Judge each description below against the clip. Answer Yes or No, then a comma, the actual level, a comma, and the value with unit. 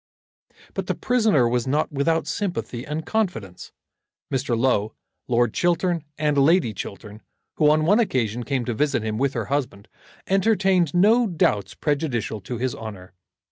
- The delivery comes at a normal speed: Yes, average, 150 wpm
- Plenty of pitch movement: Yes, wide, 6.9 semitones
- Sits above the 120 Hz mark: Yes, medium, 140 Hz